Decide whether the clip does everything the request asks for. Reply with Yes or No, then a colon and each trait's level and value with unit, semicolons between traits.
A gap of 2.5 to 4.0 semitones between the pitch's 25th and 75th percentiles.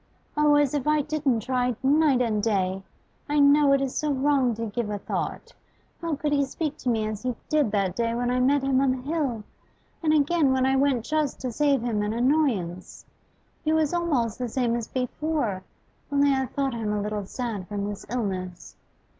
No: average, 4.6 semitones